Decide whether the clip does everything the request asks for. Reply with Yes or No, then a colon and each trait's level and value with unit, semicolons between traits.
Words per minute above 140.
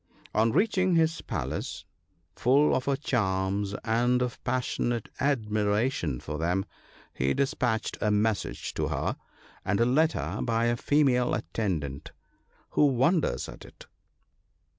No: slow, 135 wpm